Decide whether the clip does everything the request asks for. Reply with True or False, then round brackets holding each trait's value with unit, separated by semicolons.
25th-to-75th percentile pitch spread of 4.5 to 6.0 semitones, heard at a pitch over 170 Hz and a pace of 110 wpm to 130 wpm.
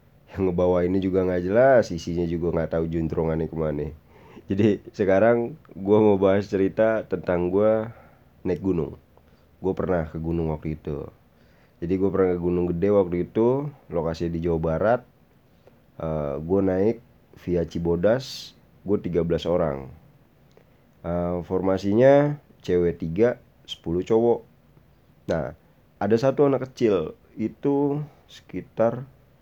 False (5.2 semitones; 95 Hz; 125 wpm)